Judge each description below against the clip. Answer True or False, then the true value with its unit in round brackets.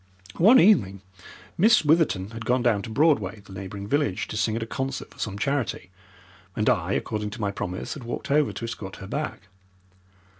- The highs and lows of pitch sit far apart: True (6.0 semitones)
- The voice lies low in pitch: True (115 Hz)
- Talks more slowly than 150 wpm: False (190 wpm)